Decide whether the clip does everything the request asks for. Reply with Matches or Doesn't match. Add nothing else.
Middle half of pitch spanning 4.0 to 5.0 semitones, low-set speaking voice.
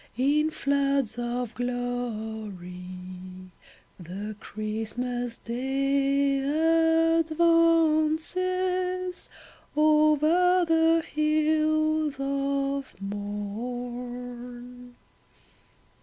Doesn't match